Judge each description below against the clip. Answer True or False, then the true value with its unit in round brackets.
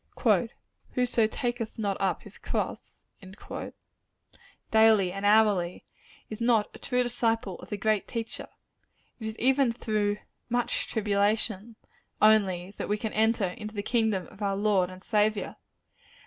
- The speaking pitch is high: True (215 Hz)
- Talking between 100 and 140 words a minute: True (135 wpm)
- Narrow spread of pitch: True (2.1 semitones)